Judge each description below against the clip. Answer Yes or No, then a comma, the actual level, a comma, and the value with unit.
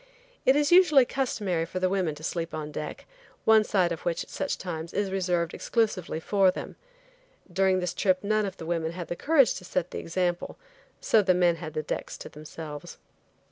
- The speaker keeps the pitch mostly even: No, average, 3.5 semitones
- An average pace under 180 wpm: No, average, 200 wpm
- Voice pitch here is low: No, medium, 180 Hz